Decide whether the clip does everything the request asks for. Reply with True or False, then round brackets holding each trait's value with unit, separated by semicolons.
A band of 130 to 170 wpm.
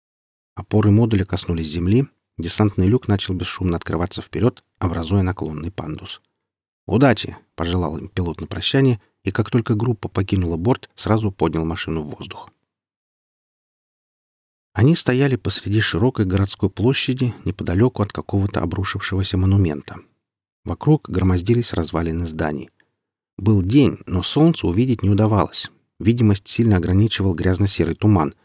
False (120 wpm)